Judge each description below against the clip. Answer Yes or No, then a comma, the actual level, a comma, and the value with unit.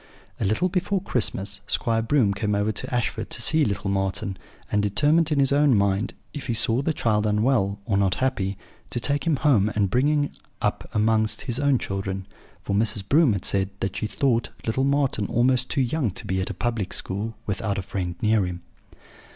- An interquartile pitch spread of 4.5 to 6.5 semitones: Yes, average, 5.2 semitones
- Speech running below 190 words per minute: No, average, 200 wpm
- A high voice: No, low, 110 Hz